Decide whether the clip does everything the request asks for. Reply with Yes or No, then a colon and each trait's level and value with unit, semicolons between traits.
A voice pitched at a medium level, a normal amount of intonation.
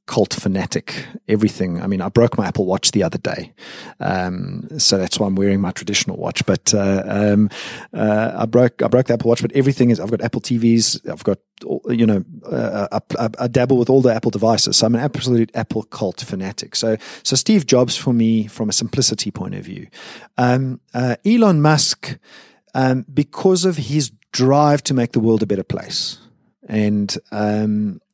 No: low, 115 Hz; average, 3.6 semitones